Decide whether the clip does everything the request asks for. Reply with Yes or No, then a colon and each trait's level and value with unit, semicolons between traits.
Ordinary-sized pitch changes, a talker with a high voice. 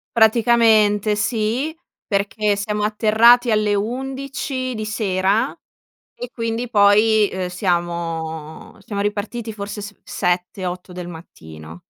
Yes: average, 3.5 semitones; high, 210 Hz